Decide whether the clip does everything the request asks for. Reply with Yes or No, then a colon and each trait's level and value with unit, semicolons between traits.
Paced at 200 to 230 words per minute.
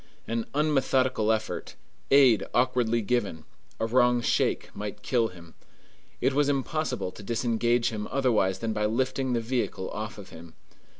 No: average, 145 wpm